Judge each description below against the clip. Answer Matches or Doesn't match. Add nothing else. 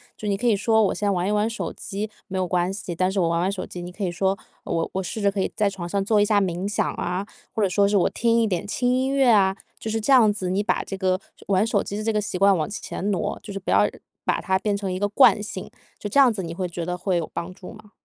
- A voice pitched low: Doesn't match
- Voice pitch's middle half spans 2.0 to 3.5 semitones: Matches